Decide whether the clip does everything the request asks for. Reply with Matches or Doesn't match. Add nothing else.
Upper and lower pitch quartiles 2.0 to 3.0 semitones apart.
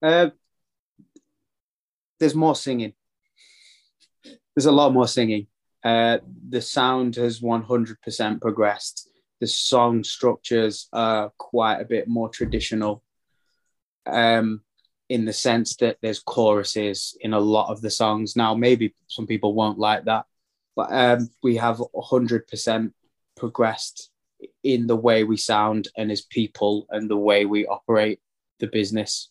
Matches